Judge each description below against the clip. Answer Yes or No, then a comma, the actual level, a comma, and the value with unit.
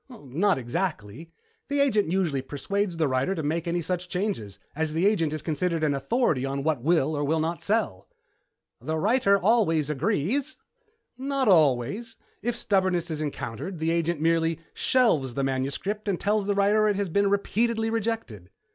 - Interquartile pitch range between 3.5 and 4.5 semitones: No, wide, 5.6 semitones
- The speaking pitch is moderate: Yes, medium, 170 Hz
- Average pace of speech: Yes, average, 165 wpm